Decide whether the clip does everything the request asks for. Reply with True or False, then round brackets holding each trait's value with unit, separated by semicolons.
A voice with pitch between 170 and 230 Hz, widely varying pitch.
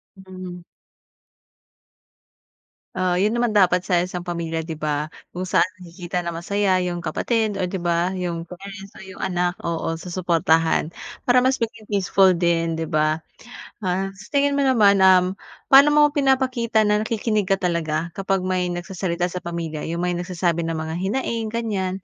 False (185 Hz; 3.1 semitones)